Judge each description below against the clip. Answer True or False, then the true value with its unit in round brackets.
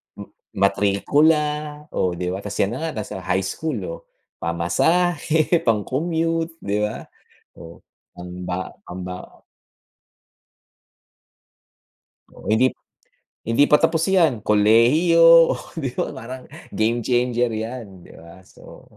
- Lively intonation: True (7.9 semitones)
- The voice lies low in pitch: True (120 Hz)